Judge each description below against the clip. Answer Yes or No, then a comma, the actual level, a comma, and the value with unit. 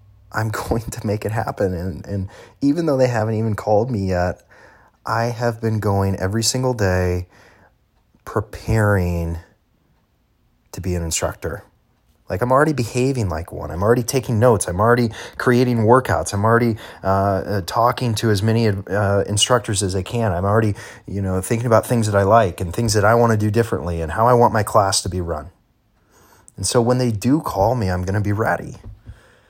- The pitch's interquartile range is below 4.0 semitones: Yes, average, 3.4 semitones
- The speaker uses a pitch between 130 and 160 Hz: No, low, 105 Hz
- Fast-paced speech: No, average, 190 wpm